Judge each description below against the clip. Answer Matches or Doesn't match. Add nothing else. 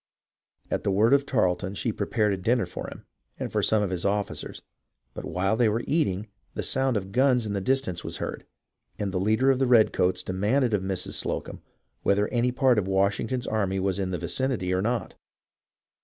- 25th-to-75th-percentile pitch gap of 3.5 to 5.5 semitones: Matches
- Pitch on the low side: Matches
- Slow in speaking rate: Doesn't match